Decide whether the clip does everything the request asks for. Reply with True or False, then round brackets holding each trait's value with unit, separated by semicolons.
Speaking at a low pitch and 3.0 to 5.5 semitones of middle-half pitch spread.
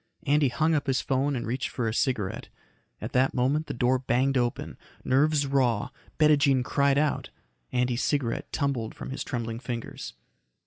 False (130 Hz; 2.6 semitones)